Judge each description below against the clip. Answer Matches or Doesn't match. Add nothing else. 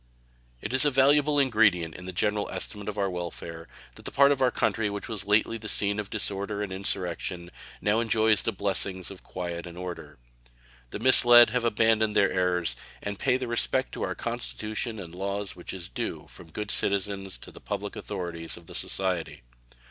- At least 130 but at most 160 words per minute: Doesn't match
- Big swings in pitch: Doesn't match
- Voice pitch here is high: Doesn't match